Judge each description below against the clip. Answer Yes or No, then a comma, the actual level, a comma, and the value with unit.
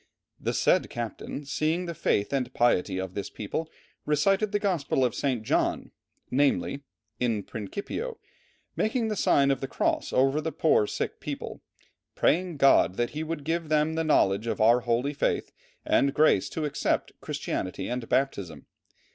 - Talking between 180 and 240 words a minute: No, average, 160 wpm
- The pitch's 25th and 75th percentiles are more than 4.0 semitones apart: Yes, wide, 5.4 semitones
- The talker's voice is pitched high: No, medium, 140 Hz